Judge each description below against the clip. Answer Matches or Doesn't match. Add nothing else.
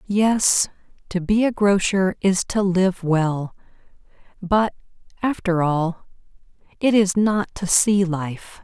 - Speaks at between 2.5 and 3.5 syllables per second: Matches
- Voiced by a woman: Matches